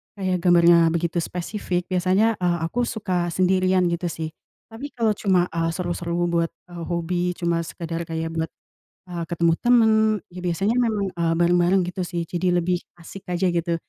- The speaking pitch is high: No, medium, 175 Hz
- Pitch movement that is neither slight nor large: No, narrow, 1.7 semitones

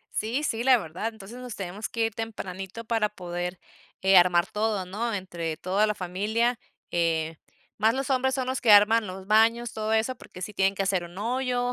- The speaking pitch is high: Yes, high, 210 Hz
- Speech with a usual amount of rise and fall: Yes, average, 3.8 semitones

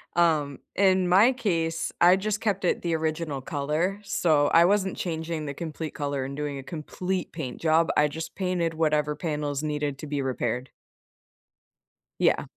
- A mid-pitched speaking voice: Yes, medium, 160 Hz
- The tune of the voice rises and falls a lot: No, average, 3.4 semitones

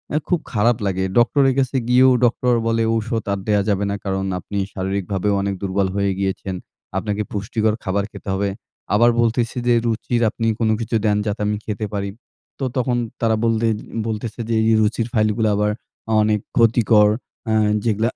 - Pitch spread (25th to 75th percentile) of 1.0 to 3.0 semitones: Yes, narrow, 2.4 semitones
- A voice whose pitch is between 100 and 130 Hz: Yes, low, 110 Hz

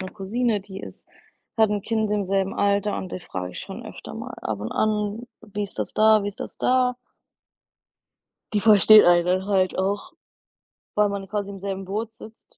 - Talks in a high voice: Yes, high, 200 Hz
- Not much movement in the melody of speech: Yes, narrow, 2.0 semitones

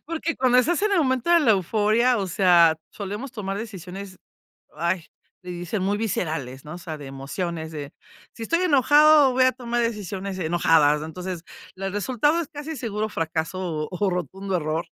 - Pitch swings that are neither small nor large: No, wide, 6.5 semitones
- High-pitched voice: Yes, high, 195 Hz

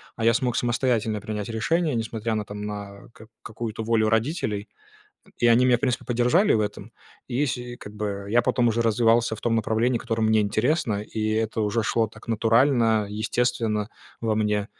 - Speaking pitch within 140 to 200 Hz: No, low, 115 Hz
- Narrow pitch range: Yes, narrow, 2.0 semitones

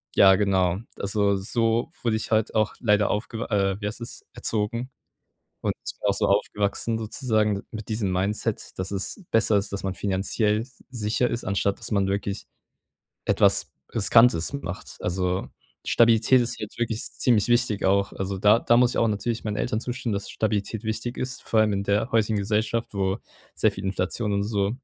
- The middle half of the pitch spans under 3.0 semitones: Yes, narrow, 2.5 semitones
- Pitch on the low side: Yes, low, 105 Hz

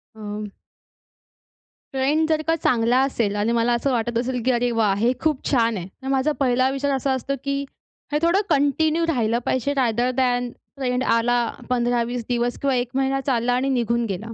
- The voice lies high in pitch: Yes, high, 245 Hz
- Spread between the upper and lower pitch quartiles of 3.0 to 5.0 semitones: No, narrow, 2.5 semitones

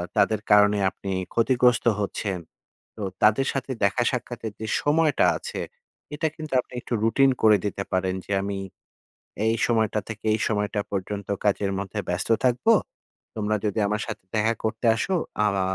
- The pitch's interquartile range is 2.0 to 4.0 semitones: Yes, average, 3.0 semitones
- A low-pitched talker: Yes, low, 110 Hz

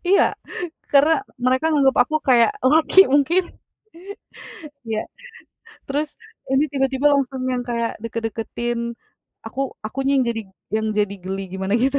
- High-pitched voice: Yes, very high, 265 Hz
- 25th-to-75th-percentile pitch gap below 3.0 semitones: No, average, 3.8 semitones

